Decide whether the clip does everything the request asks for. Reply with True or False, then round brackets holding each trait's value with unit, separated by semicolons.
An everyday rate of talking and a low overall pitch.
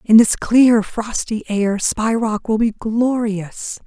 False (155 wpm; 220 Hz)